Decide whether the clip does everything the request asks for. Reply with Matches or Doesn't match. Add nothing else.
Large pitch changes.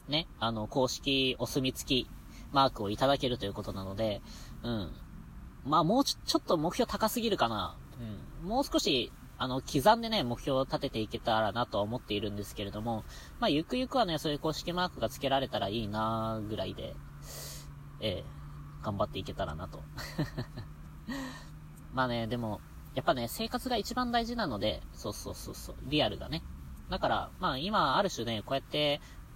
Matches